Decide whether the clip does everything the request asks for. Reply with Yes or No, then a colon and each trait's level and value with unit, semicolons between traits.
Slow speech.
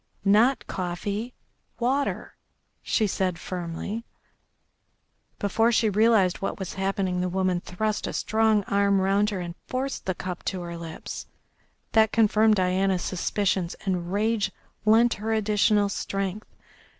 Yes: slow, 130 wpm